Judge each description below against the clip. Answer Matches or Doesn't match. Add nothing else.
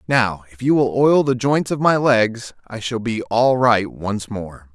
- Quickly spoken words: Matches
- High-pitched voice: Doesn't match